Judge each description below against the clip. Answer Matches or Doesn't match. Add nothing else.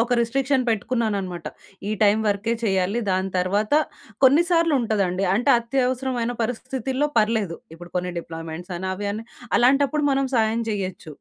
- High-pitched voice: Matches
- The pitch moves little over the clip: Doesn't match